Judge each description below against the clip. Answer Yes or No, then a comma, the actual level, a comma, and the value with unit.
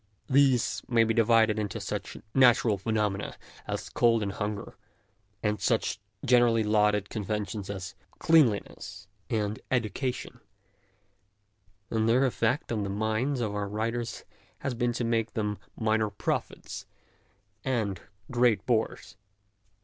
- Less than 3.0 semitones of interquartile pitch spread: Yes, narrow, 2.4 semitones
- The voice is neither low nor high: No, low, 110 Hz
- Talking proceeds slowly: Yes, slow, 120 wpm